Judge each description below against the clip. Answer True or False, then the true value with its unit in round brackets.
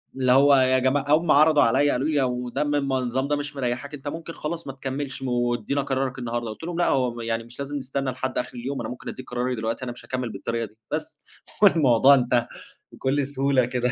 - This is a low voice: True (130 Hz)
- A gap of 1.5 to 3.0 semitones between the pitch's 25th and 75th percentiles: True (2.5 semitones)